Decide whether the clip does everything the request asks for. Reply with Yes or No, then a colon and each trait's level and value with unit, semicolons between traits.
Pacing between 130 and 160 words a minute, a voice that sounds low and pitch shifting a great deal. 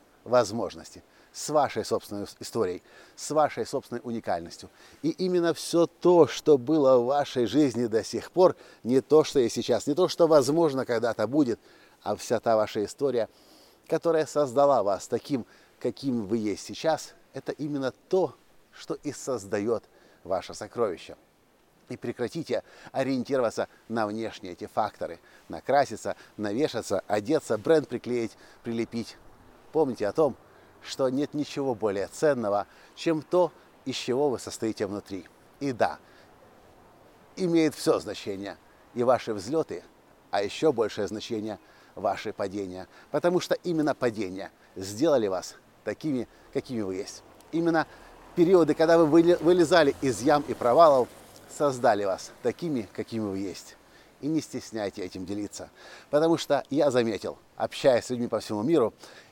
Yes: average, 135 wpm; low, 130 Hz; wide, 6.1 semitones